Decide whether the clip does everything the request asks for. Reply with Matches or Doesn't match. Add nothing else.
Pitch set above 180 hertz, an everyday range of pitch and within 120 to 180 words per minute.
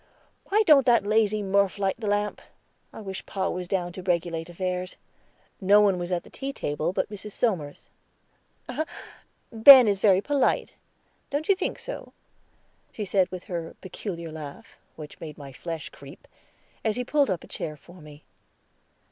Matches